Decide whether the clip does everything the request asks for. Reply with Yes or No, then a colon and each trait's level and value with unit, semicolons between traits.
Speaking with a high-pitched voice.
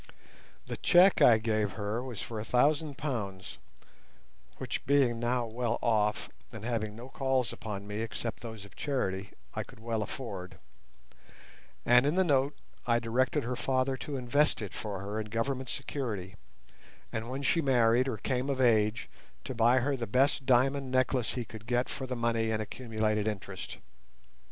No: low, 120 Hz